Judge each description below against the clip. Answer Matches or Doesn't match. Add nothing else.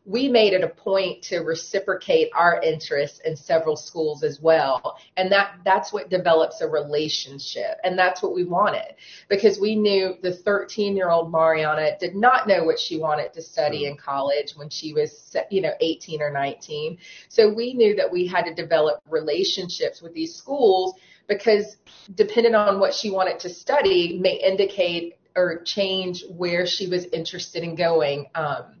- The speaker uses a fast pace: Doesn't match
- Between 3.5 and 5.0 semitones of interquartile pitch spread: Matches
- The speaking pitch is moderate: Matches